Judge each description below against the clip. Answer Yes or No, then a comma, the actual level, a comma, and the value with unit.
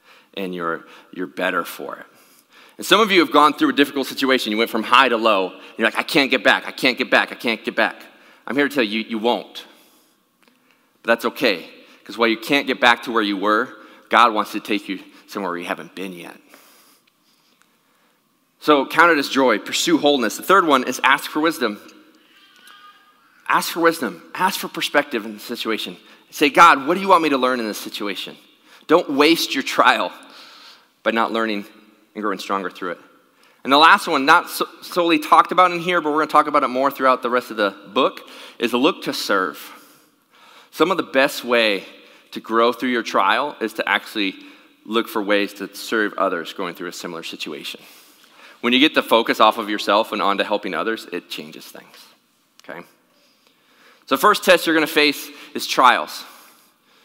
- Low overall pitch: Yes, low, 120 Hz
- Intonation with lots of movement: Yes, wide, 5.8 semitones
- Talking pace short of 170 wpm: No, fast, 205 wpm